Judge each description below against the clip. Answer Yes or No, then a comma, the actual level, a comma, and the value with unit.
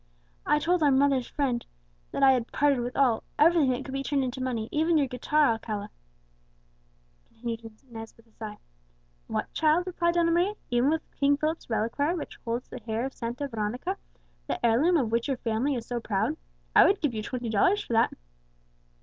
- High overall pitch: Yes, very high, 260 Hz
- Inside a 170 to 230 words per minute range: Yes, average, 190 wpm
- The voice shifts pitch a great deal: No, average, 4.5 semitones